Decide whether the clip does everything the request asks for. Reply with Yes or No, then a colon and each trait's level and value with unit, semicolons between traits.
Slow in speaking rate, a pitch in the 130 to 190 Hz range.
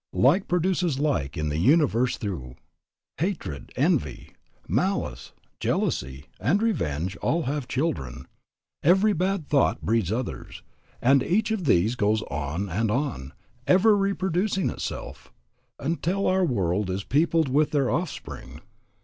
Yes: slow, 125 wpm; low, 135 Hz